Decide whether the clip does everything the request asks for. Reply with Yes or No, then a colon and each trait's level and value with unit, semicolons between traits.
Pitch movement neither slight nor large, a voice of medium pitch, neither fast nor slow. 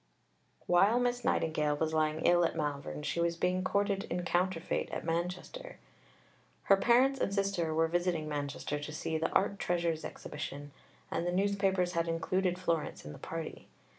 Yes: average, 3.3 semitones; medium, 175 Hz; average, 165 wpm